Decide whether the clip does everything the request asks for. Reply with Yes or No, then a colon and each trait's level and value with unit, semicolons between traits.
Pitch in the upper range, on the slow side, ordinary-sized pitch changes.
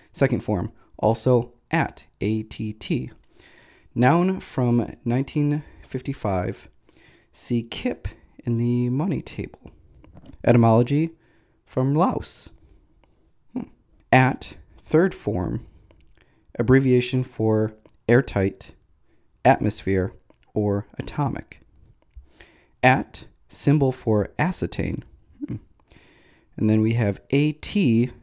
No: low, 120 Hz; slow, 85 wpm; average, 3.3 semitones